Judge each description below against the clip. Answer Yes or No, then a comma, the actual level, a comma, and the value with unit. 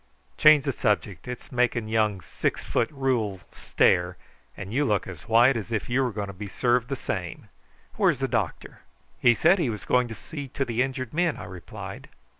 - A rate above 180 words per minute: Yes, average, 200 wpm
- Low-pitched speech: Yes, low, 120 Hz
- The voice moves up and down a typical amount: Yes, average, 4.2 semitones